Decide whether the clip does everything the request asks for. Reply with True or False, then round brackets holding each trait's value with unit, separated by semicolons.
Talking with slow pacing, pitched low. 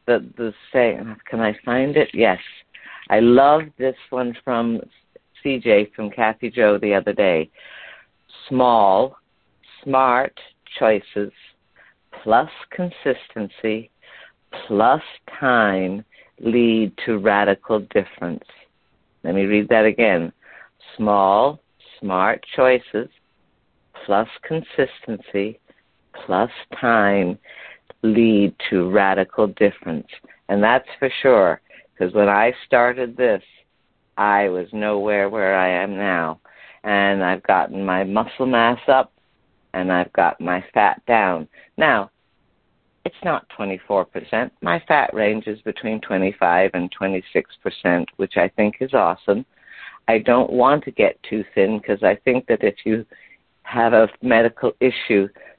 True (120 wpm; 110 Hz)